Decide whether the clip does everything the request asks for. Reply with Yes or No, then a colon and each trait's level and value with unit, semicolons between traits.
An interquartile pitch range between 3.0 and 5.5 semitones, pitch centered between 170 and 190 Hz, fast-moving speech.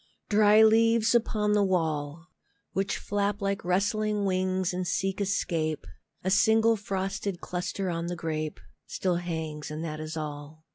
No: average, 4.1 semitones; medium, 185 Hz; average, 145 wpm